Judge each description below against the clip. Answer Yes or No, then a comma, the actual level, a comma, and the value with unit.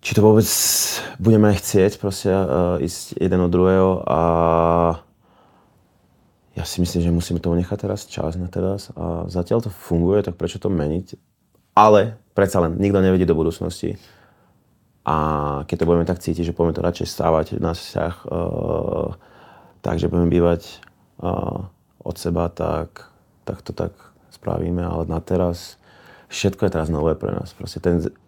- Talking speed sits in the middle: Yes, average, 155 wpm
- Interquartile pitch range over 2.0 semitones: Yes, narrow, 2.4 semitones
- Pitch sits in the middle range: No, very low, 90 Hz